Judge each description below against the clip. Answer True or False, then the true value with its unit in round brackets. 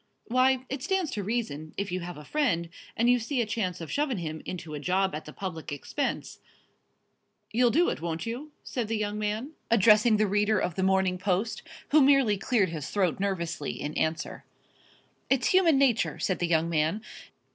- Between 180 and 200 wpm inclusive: True (190 wpm)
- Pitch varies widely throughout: True (6.2 semitones)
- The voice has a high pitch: True (205 Hz)